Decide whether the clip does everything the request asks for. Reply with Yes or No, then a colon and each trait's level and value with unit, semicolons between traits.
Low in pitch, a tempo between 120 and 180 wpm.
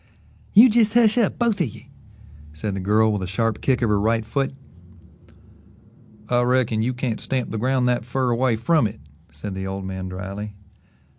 No: low, 115 Hz; average, 190 wpm